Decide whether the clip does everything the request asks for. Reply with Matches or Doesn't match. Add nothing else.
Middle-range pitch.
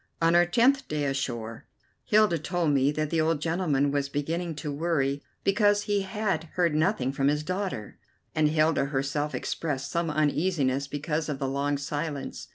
Matches